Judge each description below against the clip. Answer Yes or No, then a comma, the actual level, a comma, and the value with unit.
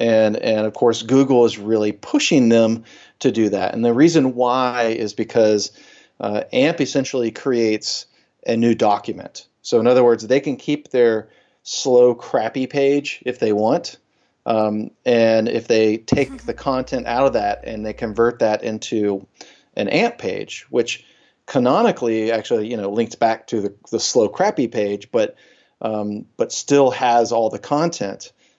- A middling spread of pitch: Yes, average, 3.1 semitones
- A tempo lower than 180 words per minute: Yes, average, 165 wpm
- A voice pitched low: Yes, low, 115 Hz